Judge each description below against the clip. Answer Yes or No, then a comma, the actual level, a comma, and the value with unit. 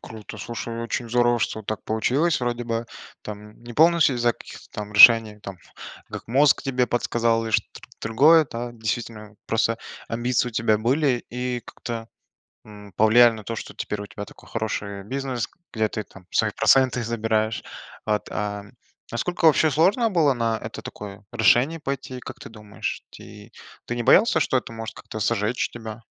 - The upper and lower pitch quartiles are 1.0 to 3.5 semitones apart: Yes, narrow, 2.5 semitones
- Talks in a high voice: No, low, 115 Hz